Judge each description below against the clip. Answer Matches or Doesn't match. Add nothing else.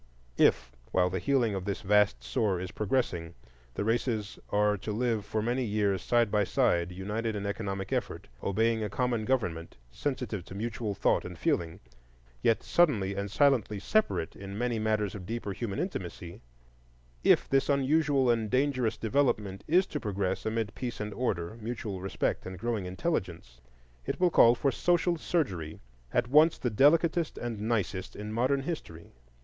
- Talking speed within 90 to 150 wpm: Doesn't match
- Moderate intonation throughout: Matches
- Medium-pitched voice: Doesn't match